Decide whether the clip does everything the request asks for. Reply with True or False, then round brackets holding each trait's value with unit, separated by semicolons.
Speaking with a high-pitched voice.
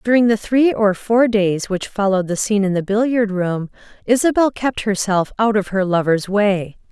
True (210 Hz)